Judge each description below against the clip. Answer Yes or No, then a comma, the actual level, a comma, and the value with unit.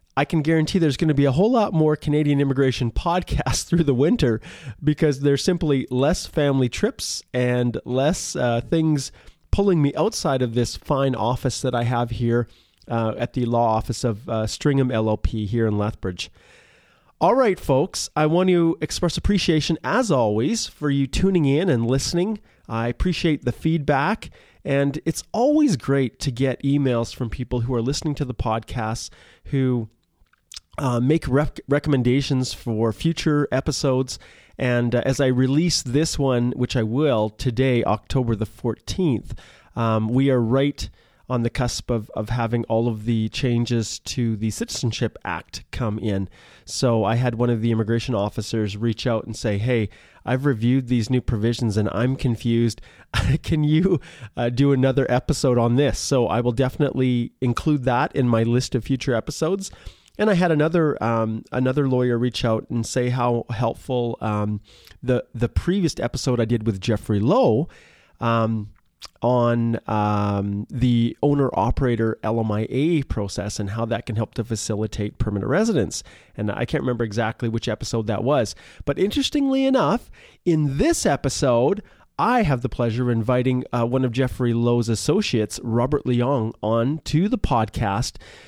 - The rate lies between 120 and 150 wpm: No, average, 165 wpm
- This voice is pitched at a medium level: No, low, 125 Hz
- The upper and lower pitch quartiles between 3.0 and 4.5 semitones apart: Yes, average, 3.8 semitones